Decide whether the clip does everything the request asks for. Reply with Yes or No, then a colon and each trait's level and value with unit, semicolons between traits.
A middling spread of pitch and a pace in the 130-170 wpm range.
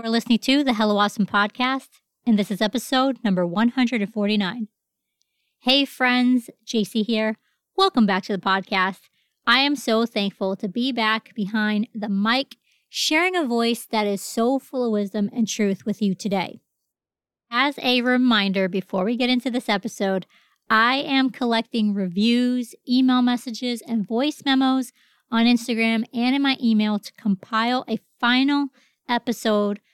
Yes: average, 3.1 semitones; average, 150 wpm